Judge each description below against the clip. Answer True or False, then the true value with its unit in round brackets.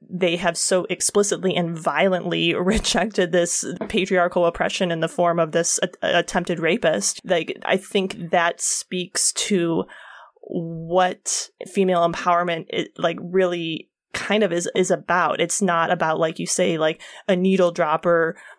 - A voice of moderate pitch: True (175 Hz)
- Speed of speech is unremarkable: True (145 wpm)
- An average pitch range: False (1.8 semitones)